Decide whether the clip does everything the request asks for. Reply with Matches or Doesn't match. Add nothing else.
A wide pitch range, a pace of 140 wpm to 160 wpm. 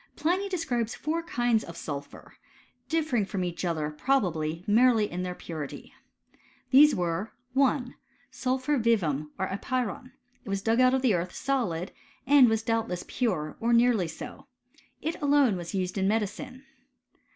Matches